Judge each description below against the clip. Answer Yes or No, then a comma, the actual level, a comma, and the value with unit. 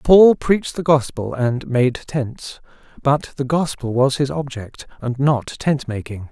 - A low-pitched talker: Yes, low, 130 Hz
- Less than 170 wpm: Yes, average, 160 wpm